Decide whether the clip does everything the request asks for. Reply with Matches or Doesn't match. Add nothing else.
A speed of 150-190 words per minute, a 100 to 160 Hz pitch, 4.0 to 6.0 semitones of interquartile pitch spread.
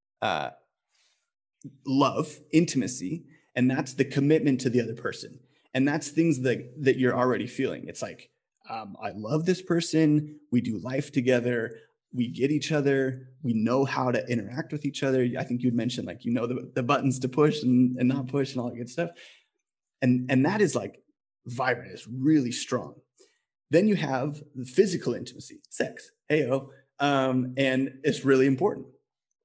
Doesn't match